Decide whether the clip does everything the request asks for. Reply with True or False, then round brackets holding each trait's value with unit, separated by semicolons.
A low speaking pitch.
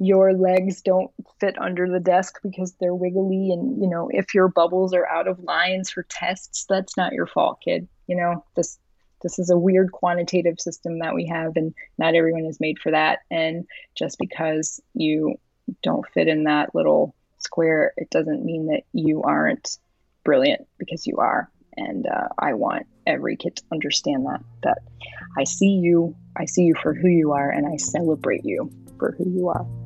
False (175 Hz)